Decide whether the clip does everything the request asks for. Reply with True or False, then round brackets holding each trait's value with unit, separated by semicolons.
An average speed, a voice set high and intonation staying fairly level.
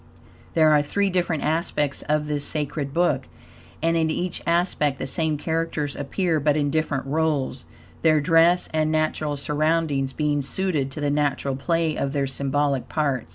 False (160 wpm; 150 Hz; 2.3 semitones)